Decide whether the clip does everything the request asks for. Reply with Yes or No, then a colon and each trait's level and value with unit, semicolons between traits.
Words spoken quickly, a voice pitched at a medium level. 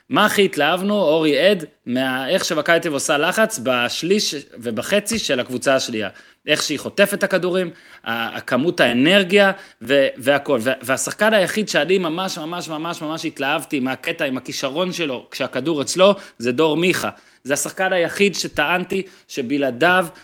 No: average, 135 wpm; medium, 170 Hz